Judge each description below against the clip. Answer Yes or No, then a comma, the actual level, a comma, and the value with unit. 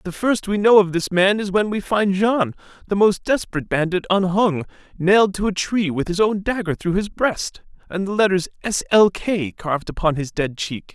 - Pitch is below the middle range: No, high, 190 Hz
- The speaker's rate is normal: No, fast, 215 wpm